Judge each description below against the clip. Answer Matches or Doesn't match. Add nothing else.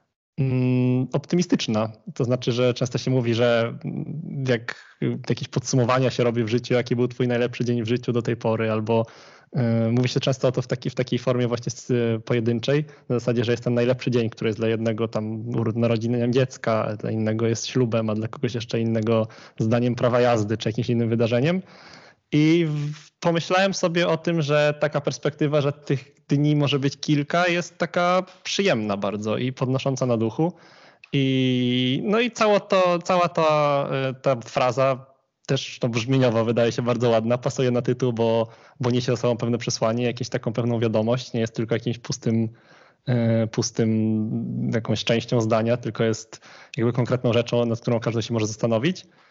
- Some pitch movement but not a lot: Matches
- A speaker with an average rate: Doesn't match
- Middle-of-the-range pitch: Doesn't match